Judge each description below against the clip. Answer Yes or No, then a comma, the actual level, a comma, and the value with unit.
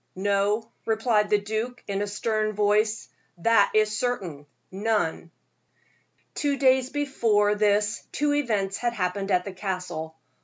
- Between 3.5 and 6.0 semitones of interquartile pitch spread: No, narrow, 2.6 semitones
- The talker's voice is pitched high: Yes, high, 210 Hz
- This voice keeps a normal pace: No, slow, 130 wpm